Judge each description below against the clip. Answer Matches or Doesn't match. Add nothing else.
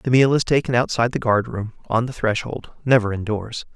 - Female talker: Doesn't match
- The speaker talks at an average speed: Doesn't match